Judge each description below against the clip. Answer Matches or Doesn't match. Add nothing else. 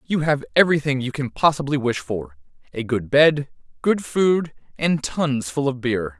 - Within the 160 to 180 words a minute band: Matches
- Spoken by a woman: Doesn't match